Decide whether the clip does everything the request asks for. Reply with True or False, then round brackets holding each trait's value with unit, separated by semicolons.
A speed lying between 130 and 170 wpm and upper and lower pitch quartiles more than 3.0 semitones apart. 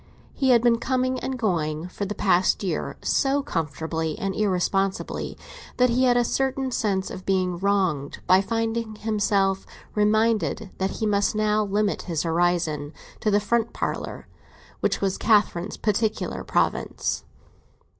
True (145 wpm; 3.8 semitones)